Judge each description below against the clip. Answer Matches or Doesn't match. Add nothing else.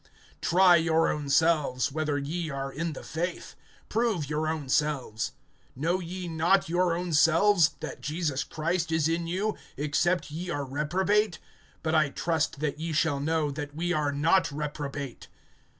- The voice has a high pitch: Doesn't match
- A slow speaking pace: Doesn't match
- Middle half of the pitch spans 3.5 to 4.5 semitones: Doesn't match